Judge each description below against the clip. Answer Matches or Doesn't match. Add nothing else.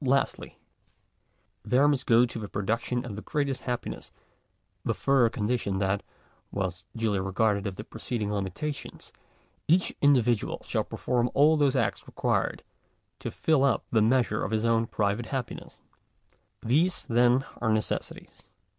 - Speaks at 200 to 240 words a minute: Doesn't match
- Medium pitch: Doesn't match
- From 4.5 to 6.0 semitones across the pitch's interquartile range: Doesn't match